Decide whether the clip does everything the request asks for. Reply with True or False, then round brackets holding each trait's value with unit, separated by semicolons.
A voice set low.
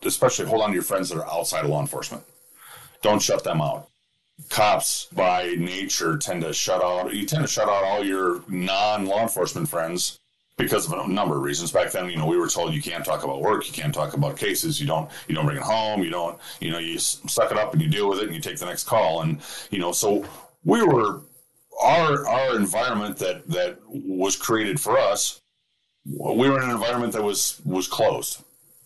True (100 Hz)